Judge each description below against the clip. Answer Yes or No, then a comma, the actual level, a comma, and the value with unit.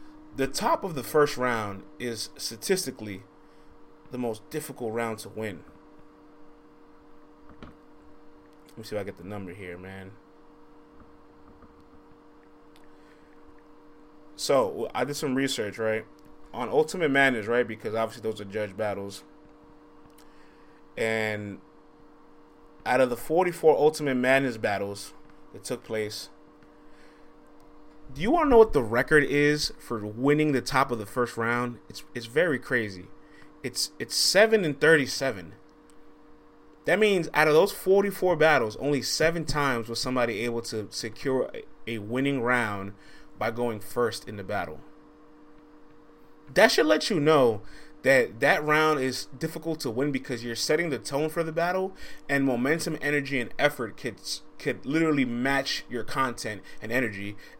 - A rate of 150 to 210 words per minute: No, average, 140 wpm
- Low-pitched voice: No, medium, 145 Hz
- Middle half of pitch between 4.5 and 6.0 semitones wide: Yes, average, 4.9 semitones